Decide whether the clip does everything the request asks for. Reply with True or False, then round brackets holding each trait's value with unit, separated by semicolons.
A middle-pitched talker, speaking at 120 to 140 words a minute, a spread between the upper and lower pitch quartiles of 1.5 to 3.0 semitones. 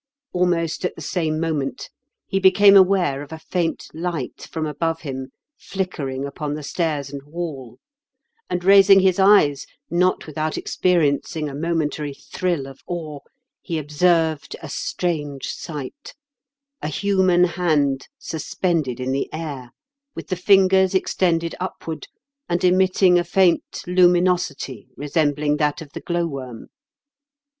False (165 Hz; 135 wpm; 3.7 semitones)